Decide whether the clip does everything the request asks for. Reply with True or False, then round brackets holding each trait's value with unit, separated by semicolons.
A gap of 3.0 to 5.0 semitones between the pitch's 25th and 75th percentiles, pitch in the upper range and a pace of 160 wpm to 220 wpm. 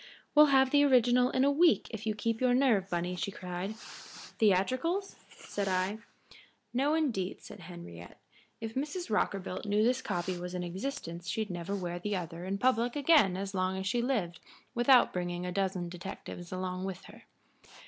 False (5.6 semitones; 200 Hz; 175 wpm)